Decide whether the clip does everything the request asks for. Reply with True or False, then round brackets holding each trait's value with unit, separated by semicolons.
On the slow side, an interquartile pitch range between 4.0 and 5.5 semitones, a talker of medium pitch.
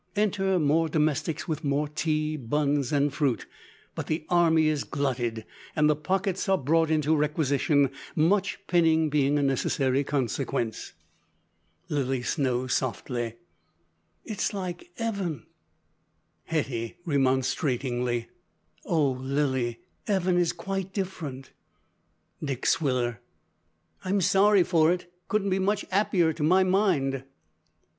True (115 wpm; 4.6 semitones; 150 Hz)